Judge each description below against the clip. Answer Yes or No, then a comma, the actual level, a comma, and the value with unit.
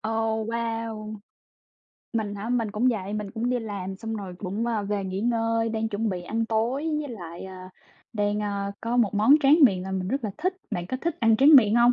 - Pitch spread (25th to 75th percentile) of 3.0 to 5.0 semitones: No, narrow, 2.6 semitones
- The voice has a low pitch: No, high, 220 Hz